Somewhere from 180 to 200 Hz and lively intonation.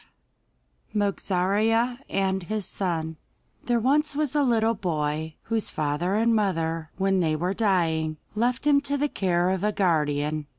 Yes: high, 190 Hz; wide, 5.9 semitones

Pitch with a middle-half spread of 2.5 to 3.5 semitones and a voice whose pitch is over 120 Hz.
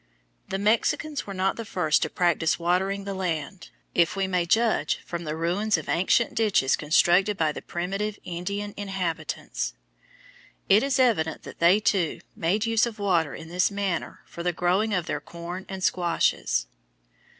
Yes: average, 3.1 semitones; medium, 185 Hz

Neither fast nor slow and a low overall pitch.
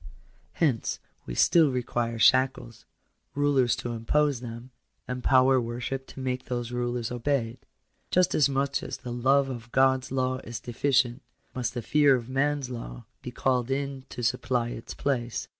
Yes: average, 160 wpm; low, 125 Hz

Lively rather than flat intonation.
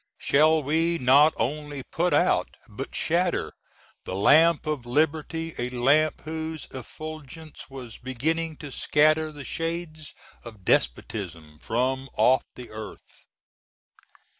No: average, 4.0 semitones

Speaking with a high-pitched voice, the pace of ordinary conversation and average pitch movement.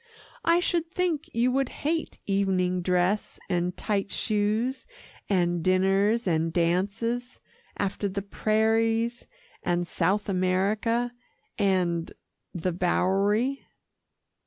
No: high, 200 Hz; slow, 100 wpm; average, 4.2 semitones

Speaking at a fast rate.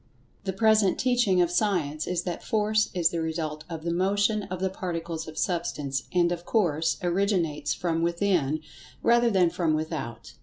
No: average, 165 wpm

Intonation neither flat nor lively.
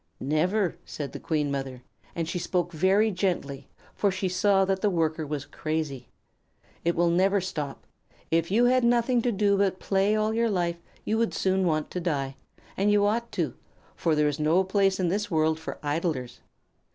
Yes: average, 4.5 semitones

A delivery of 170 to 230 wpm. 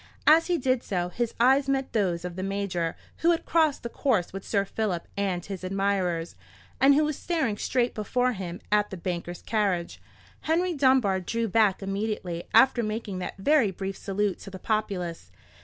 Yes: average, 180 wpm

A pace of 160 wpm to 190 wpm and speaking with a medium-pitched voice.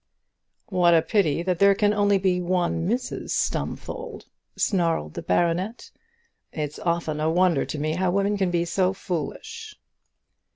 No: average, 150 wpm; medium, 180 Hz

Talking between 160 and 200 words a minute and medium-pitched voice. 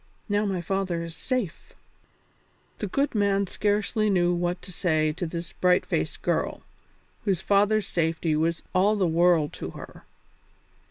No: average, 150 wpm; medium, 180 Hz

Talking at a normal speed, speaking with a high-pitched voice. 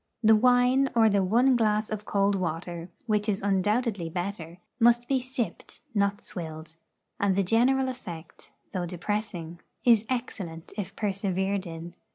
Yes: average, 145 wpm; high, 200 Hz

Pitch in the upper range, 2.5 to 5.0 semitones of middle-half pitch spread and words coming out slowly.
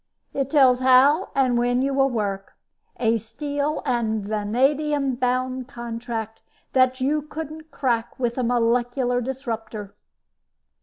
Yes: very high, 250 Hz; average, 2.9 semitones; slow, 120 wpm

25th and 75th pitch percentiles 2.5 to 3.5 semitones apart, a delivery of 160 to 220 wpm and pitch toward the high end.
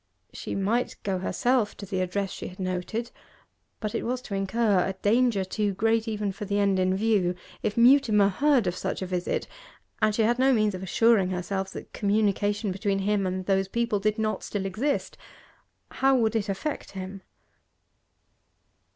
Yes: average, 2.9 semitones; average, 175 wpm; high, 205 Hz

